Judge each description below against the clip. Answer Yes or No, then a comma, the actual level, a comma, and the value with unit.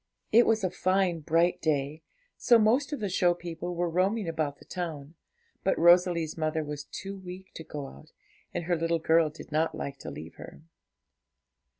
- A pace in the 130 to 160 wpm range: No, average, 185 wpm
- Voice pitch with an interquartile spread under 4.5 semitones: Yes, average, 3.1 semitones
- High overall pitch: No, medium, 170 Hz